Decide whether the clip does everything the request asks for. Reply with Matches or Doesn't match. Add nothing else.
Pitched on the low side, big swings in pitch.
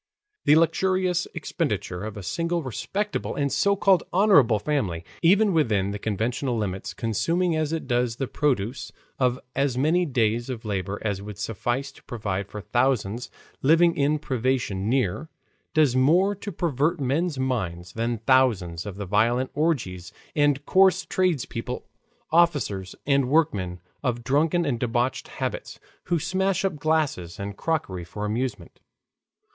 Matches